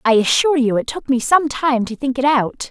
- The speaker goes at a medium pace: No, fast, 265 wpm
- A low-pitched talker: No, very high, 260 Hz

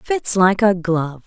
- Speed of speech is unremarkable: Yes, average, 190 wpm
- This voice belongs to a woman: Yes, female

